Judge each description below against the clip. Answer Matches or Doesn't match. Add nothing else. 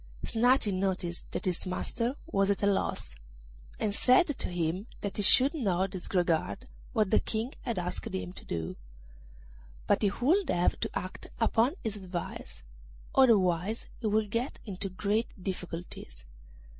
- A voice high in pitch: Matches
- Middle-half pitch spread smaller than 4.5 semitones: Matches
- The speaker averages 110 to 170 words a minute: Matches